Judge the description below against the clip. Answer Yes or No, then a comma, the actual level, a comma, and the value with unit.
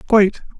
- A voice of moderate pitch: No, high, 210 Hz